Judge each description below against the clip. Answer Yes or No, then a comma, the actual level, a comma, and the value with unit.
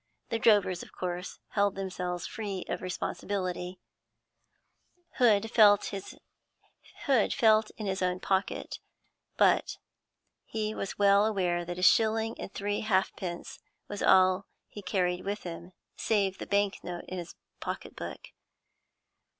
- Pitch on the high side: Yes, high, 195 Hz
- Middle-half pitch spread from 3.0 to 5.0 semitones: No, narrow, 2.5 semitones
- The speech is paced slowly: Yes, slow, 125 wpm